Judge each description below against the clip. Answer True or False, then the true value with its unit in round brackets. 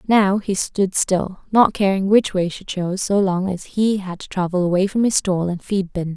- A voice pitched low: False (190 Hz)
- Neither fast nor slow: False (235 wpm)